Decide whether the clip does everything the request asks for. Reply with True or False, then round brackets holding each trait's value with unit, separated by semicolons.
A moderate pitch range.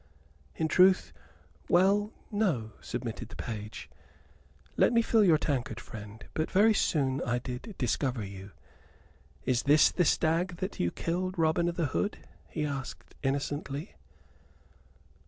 False (6.8 semitones)